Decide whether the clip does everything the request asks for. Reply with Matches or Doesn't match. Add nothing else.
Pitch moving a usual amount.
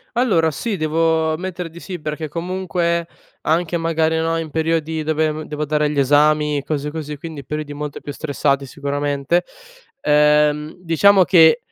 Doesn't match